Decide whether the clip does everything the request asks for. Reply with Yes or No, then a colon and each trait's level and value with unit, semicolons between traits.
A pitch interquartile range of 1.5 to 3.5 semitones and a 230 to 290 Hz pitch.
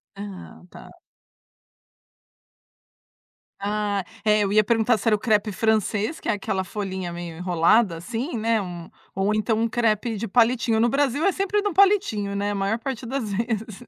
No: average, 2.9 semitones; high, 215 Hz